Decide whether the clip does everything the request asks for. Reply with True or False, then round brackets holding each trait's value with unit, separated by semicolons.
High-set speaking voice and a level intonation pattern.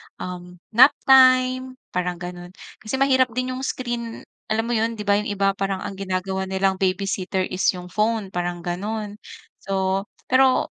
False (200 Hz; 4.0 semitones)